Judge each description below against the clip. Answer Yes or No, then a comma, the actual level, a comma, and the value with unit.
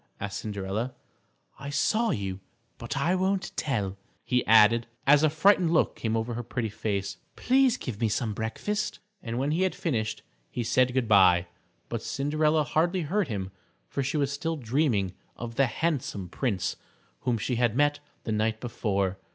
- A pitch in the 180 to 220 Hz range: No, low, 120 Hz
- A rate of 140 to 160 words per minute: No, average, 170 wpm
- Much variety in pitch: Yes, wide, 6.0 semitones